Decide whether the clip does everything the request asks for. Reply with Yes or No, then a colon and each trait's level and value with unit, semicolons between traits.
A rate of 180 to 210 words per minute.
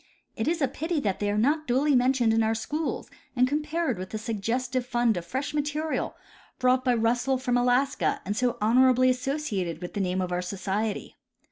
Yes: average, 200 wpm